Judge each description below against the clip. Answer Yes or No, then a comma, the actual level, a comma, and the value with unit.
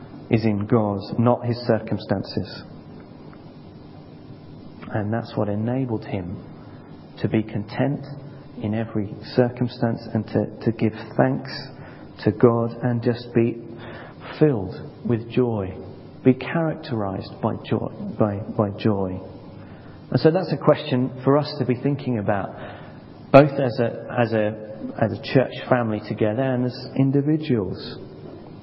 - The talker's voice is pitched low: Yes, low, 115 Hz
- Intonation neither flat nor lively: Yes, average, 3.3 semitones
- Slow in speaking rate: Yes, slow, 130 wpm